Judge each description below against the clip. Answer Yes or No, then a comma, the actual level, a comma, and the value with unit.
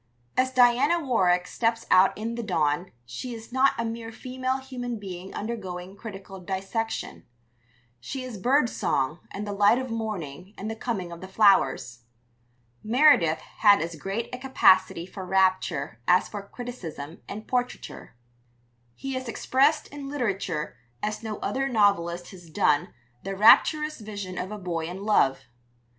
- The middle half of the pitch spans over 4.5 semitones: Yes, average, 5.1 semitones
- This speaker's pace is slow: No, average, 150 wpm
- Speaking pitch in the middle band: No, high, 205 Hz